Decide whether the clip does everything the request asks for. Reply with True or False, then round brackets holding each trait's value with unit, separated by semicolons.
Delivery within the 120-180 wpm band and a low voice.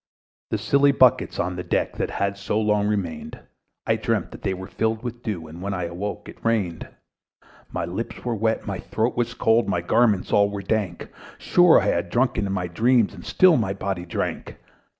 False (200 wpm; 100 Hz)